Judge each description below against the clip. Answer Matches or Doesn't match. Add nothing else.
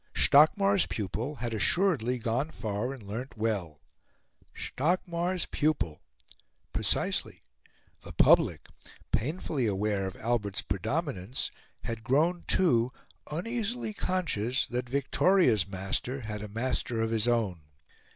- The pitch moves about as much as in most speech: Doesn't match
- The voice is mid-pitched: Doesn't match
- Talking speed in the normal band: Doesn't match